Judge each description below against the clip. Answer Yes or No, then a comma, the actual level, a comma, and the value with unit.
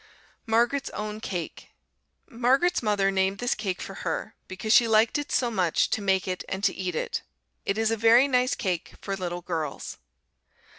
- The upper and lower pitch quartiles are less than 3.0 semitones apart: No, average, 3.9 semitones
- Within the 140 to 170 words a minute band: No, average, 180 wpm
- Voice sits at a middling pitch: No, high, 210 Hz